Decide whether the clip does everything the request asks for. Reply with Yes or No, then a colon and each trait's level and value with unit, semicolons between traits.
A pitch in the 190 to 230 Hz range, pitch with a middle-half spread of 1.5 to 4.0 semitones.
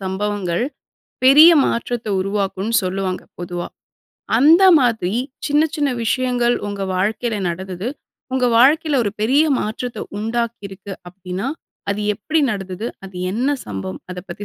No: high, 210 Hz; average, 4.6 semitones